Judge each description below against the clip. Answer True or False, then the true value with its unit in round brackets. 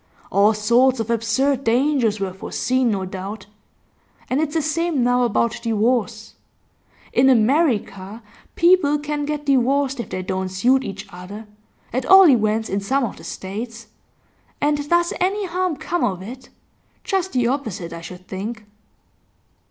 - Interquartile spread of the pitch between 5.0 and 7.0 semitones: True (5.5 semitones)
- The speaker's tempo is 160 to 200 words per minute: False (150 wpm)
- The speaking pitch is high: True (240 Hz)